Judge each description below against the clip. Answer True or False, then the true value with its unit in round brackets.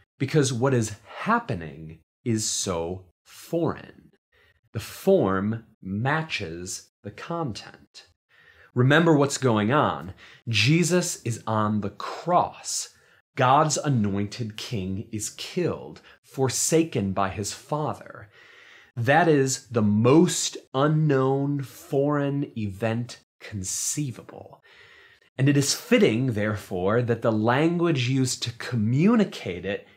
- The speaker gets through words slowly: True (100 wpm)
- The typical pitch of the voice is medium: False (120 Hz)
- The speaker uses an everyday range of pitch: False (5.7 semitones)